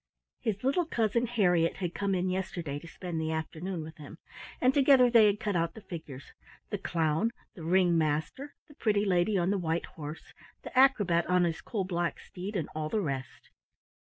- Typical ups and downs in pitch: Yes, average, 4.5 semitones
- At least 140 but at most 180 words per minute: No, average, 195 wpm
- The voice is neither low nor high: Yes, medium, 180 Hz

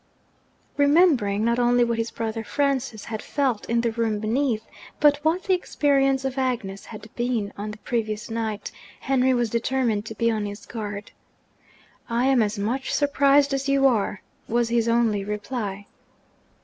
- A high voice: Yes, high, 235 Hz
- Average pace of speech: Yes, average, 160 wpm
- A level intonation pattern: No, average, 3.8 semitones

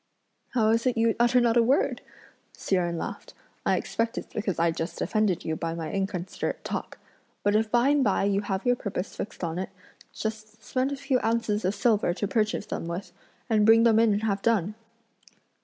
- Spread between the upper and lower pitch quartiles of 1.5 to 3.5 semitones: Yes, average, 3.2 semitones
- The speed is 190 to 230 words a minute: Yes, fast, 205 wpm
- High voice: Yes, high, 215 Hz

